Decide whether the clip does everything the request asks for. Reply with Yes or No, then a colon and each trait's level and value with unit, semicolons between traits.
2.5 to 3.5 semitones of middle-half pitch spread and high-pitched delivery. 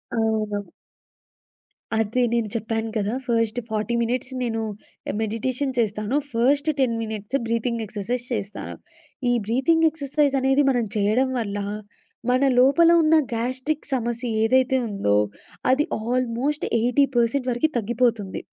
Yes: average, 2.9 semitones; high, 235 Hz